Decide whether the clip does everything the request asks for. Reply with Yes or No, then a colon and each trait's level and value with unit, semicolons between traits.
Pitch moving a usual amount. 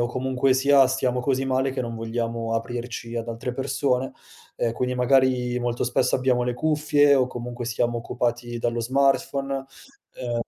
No: narrow, 1.9 semitones